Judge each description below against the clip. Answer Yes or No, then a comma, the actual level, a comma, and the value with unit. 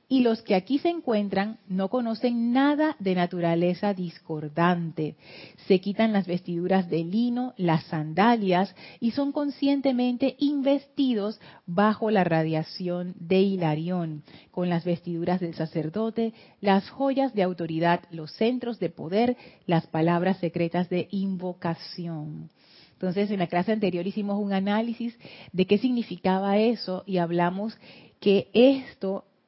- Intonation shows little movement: No, average, 4.7 semitones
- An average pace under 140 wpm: Yes, average, 130 wpm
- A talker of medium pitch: No, high, 195 Hz